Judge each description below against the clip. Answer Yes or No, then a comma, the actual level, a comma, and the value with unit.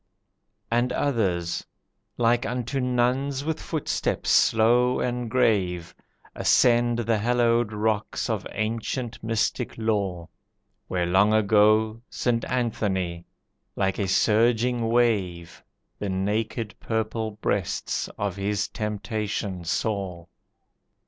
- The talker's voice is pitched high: No, low, 110 Hz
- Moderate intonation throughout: Yes, average, 3.2 semitones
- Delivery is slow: Yes, slow, 100 wpm